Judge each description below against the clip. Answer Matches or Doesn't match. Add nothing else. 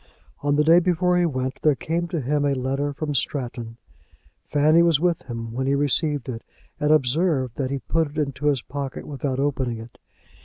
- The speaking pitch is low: Doesn't match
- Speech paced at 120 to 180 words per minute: Doesn't match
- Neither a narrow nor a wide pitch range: Matches